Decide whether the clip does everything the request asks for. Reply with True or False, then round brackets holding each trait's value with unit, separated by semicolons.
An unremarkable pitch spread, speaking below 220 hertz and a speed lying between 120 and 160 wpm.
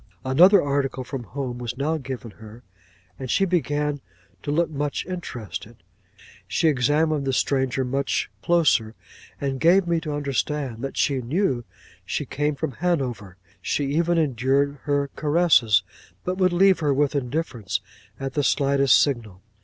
True (3.6 semitones; 140 Hz; 145 wpm)